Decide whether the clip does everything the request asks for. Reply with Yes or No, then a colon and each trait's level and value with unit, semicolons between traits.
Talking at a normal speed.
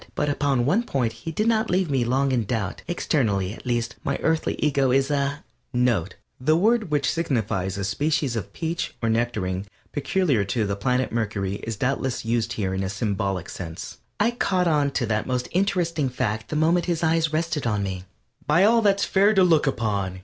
Yes: average, 195 wpm